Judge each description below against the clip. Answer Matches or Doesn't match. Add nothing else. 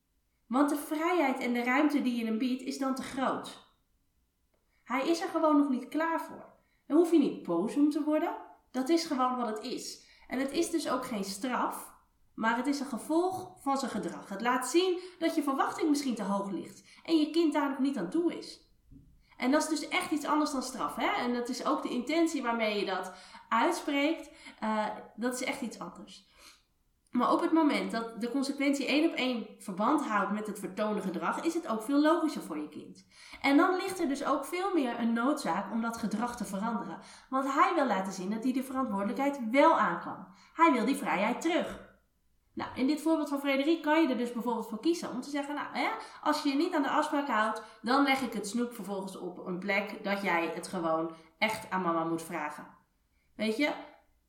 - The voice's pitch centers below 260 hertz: Doesn't match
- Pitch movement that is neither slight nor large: Doesn't match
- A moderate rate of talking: Doesn't match